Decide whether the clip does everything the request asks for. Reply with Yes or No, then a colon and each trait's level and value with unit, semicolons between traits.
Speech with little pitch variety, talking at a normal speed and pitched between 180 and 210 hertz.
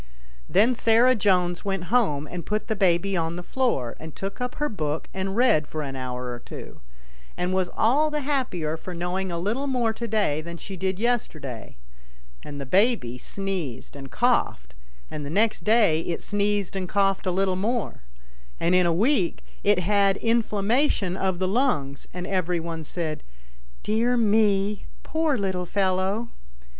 No: average, 4.7 semitones; average, 170 wpm; high, 190 Hz